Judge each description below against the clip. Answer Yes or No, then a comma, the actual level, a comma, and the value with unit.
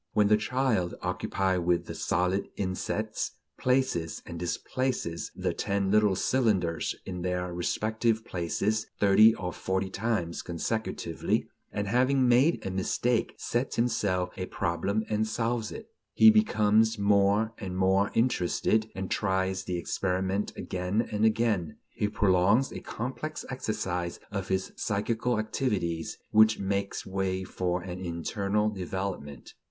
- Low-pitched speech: Yes, low, 100 Hz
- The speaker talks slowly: Yes, slow, 130 wpm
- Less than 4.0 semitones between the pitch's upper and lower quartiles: Yes, average, 3.4 semitones